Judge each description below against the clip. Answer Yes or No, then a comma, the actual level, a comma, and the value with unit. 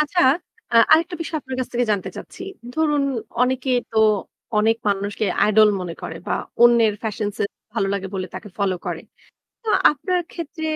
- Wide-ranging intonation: Yes, wide, 6.8 semitones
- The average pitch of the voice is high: Yes, high, 235 Hz